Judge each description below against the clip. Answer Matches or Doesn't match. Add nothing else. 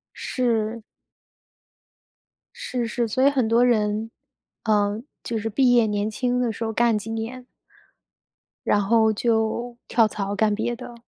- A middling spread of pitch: Doesn't match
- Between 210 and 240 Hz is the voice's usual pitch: Matches